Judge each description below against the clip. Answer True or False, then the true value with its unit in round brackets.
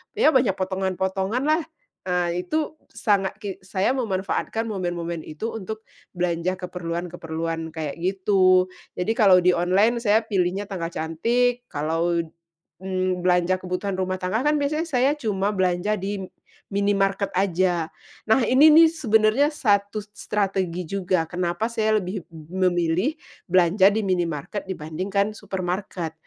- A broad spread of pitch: False (3.3 semitones)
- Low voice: False (190 Hz)